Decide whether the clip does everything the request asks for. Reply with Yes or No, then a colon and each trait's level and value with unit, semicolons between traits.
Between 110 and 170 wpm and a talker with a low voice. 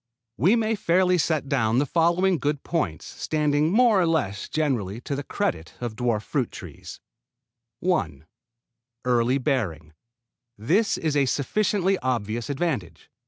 No: slow, 135 wpm; medium, 145 Hz